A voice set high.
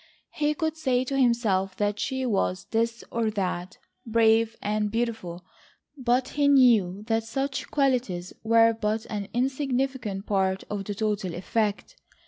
Yes: high, 225 Hz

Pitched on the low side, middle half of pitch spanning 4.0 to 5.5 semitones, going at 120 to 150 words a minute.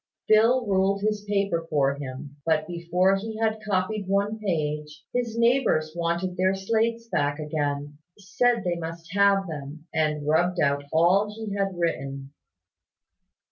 No: medium, 180 Hz; average, 5.1 semitones; average, 140 wpm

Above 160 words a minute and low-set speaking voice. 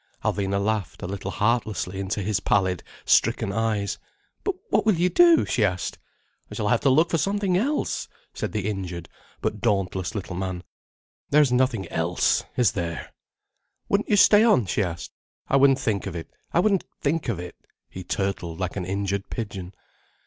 Yes: average, 175 wpm; low, 105 Hz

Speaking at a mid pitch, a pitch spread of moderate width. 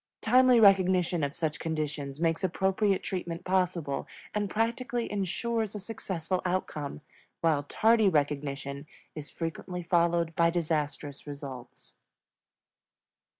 Yes: medium, 170 Hz; average, 4.4 semitones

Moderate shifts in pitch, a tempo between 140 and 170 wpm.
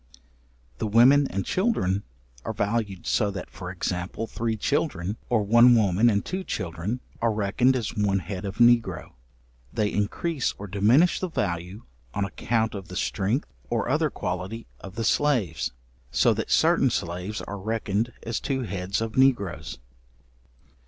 Yes: average, 3.7 semitones; average, 150 wpm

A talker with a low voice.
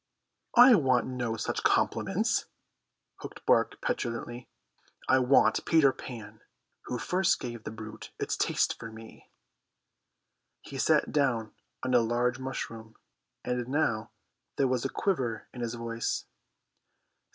Yes: low, 120 Hz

